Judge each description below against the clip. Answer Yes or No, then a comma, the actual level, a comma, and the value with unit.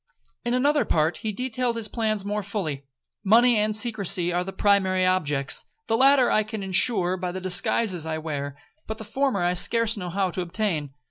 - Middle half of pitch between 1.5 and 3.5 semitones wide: No, average, 4.1 semitones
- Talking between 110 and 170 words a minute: No, average, 185 wpm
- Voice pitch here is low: No, high, 200 Hz